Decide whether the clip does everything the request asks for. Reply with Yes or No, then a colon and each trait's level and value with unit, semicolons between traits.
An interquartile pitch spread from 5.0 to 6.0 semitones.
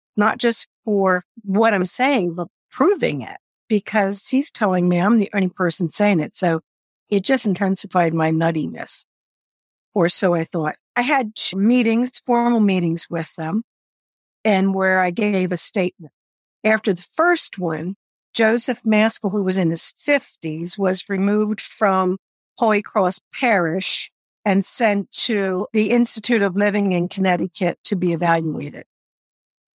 No: average, 3.6 semitones